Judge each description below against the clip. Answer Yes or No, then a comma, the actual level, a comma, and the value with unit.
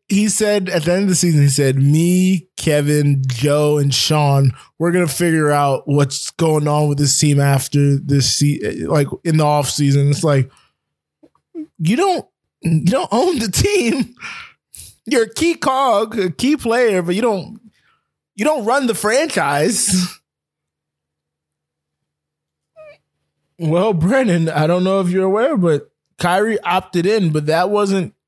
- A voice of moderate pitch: Yes, medium, 175 Hz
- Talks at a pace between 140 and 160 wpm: Yes, average, 155 wpm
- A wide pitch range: Yes, wide, 6.3 semitones